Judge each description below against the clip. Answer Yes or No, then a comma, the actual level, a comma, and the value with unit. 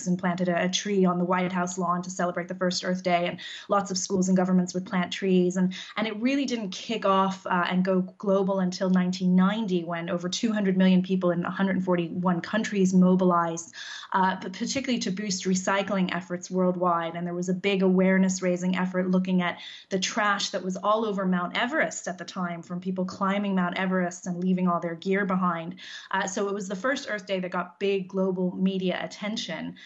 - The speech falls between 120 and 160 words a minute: No, average, 200 wpm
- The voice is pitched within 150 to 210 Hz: Yes, medium, 185 Hz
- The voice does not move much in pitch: Yes, narrow, 1.6 semitones